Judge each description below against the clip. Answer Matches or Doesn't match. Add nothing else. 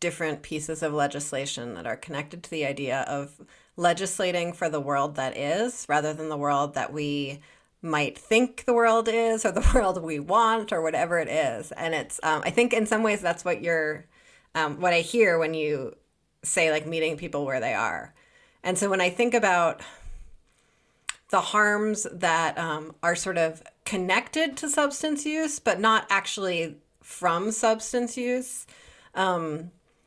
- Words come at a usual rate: Matches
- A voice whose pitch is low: Doesn't match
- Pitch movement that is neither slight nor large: Doesn't match